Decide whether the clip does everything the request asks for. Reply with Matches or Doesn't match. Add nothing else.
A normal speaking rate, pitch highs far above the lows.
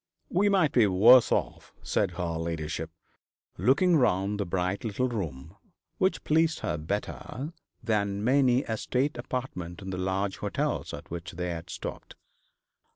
Matches